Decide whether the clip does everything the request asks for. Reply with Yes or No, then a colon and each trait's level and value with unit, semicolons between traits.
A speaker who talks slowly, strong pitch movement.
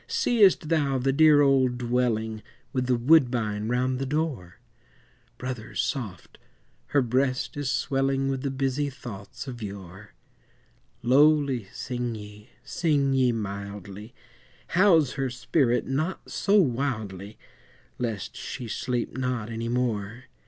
No: slow, 125 wpm; average, 3.6 semitones